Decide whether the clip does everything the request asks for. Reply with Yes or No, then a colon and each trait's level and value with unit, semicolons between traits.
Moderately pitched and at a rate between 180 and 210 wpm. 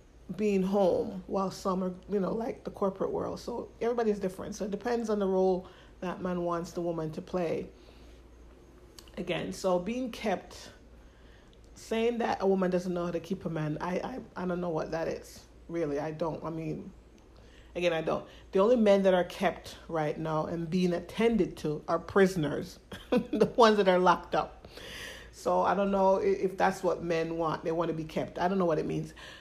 Yes: medium, 180 Hz; average, 200 wpm